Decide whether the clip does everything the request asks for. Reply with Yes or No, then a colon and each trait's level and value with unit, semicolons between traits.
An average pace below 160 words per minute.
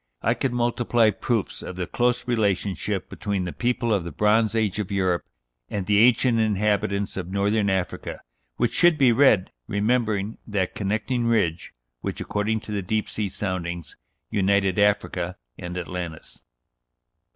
Yes: average, 150 wpm